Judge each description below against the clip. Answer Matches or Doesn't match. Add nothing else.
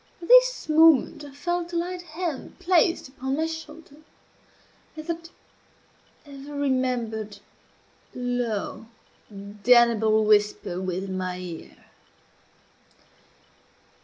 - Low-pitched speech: Doesn't match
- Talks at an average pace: Doesn't match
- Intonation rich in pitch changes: Matches